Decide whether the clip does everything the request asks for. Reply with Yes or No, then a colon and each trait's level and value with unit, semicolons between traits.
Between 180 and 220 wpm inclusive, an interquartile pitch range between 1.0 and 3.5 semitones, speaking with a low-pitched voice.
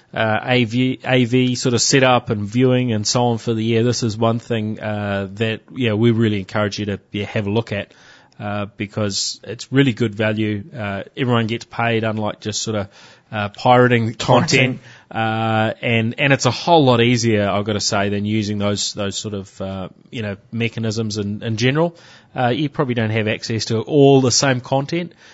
Yes: average, 200 wpm; average, 2.9 semitones; low, 115 Hz